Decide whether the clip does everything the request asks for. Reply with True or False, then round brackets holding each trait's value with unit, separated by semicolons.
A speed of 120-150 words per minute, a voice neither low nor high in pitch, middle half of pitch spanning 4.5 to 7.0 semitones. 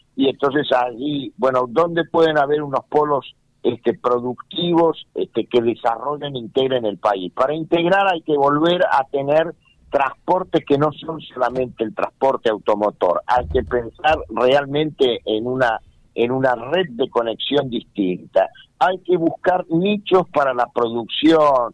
True (145 wpm; 145 Hz; 4.9 semitones)